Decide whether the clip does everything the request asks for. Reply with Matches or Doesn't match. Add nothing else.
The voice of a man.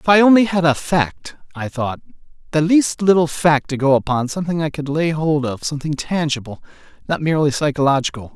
Matches